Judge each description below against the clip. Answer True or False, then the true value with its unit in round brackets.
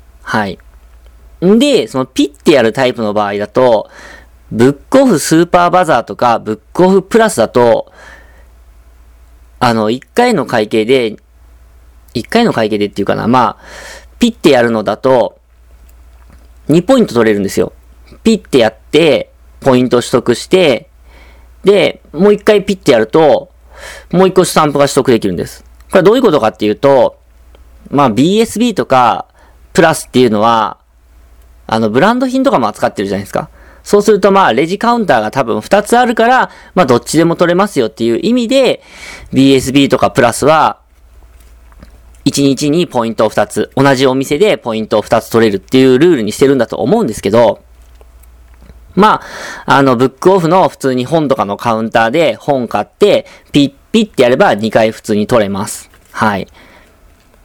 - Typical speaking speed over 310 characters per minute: True (330 characters per minute)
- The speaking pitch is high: False (115 Hz)